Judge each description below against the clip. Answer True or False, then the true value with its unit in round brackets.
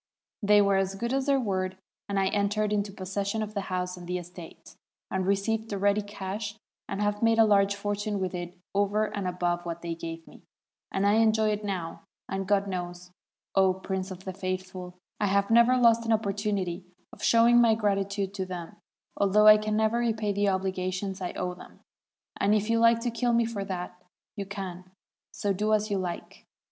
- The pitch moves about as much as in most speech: False (2.3 semitones)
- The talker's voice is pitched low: False (200 Hz)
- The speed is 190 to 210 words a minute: True (200 wpm)